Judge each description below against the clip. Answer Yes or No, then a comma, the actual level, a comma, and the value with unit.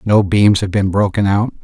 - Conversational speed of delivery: No, fast, 220 wpm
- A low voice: Yes, low, 100 Hz